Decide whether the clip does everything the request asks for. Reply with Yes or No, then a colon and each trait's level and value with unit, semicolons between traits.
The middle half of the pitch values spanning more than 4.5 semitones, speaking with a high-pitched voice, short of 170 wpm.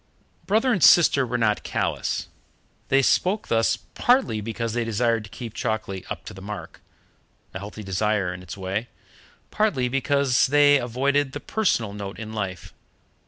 No: average, 5.2 semitones; low, 115 Hz; average, 160 wpm